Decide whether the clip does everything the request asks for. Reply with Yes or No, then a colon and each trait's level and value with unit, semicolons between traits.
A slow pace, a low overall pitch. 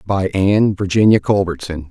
Yes: slow, 125 wpm; very low, 95 Hz